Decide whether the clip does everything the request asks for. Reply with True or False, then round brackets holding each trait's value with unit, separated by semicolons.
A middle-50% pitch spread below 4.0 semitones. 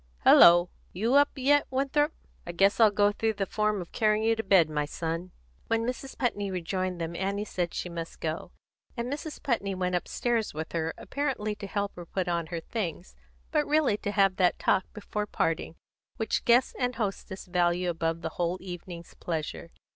False (4.6 semitones)